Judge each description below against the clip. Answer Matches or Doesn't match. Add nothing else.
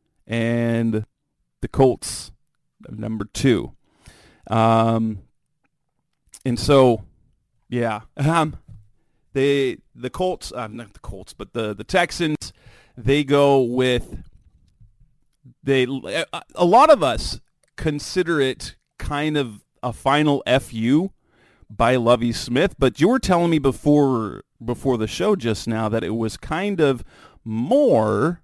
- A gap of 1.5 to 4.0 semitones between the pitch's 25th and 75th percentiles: Doesn't match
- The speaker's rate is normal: Doesn't match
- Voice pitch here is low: Matches